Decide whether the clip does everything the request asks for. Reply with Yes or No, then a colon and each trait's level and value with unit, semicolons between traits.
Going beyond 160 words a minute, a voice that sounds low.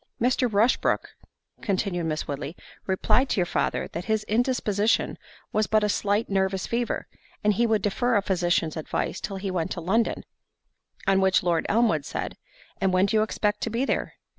No: average, 175 wpm; high, 205 Hz